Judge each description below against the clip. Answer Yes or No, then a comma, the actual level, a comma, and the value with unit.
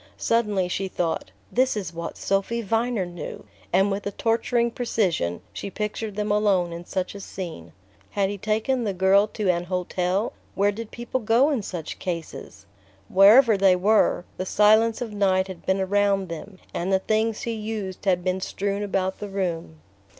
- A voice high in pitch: Yes, high, 195 Hz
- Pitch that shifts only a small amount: No, average, 3.0 semitones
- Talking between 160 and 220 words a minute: Yes, average, 170 wpm